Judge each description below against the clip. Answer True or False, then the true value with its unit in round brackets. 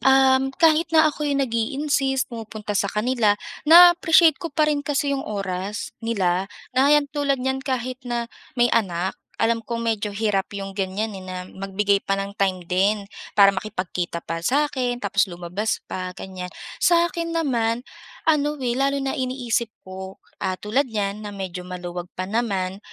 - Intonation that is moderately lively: False (5.7 semitones)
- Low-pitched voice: False (225 Hz)